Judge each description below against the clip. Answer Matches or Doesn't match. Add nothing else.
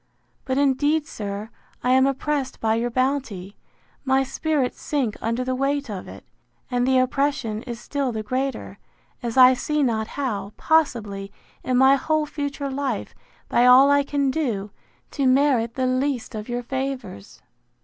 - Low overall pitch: Doesn't match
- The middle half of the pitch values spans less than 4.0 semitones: Matches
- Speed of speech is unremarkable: Matches